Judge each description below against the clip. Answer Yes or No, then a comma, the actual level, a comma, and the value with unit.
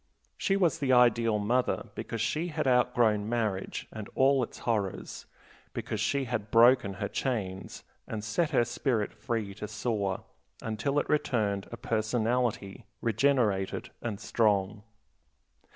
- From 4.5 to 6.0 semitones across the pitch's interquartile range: No, average, 3.2 semitones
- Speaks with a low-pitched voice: Yes, low, 115 Hz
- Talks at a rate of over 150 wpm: No, slow, 135 wpm